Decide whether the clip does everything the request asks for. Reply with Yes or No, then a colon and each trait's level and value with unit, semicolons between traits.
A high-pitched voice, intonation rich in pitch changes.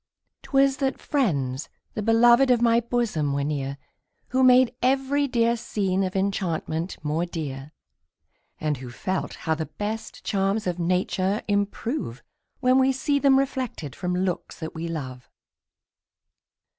Yes: high, 195 Hz; wide, 7.8 semitones